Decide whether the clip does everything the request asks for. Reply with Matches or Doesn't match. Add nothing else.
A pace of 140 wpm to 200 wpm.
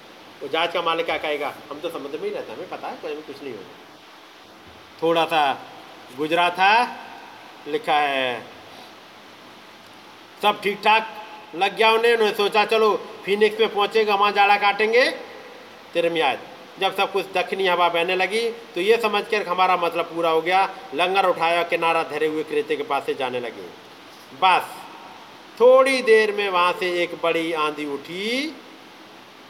Matches